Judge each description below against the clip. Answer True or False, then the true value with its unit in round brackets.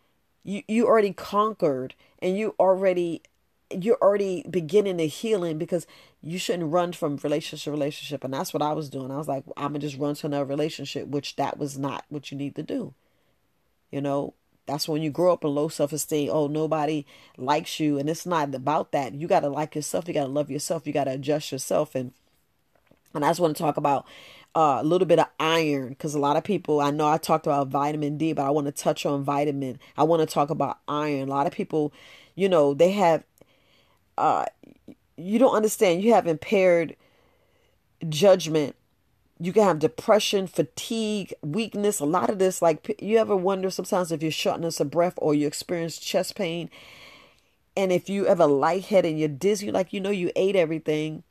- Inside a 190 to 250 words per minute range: True (200 wpm)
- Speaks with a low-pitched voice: False (155 Hz)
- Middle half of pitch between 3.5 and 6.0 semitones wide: True (3.9 semitones)